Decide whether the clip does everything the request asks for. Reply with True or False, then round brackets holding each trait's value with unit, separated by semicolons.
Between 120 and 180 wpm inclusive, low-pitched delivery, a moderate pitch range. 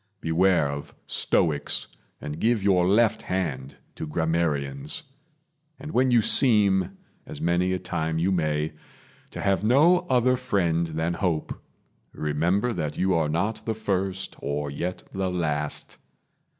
True (135 wpm; 90 Hz; 4.6 semitones)